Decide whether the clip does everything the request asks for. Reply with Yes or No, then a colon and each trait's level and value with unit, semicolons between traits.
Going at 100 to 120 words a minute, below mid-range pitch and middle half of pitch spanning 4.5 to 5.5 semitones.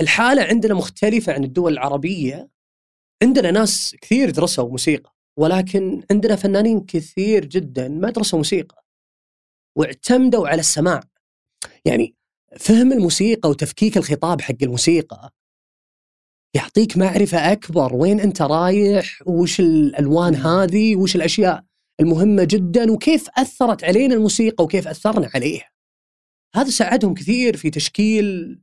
No: average, 115 wpm; high, 190 Hz; average, 4.9 semitones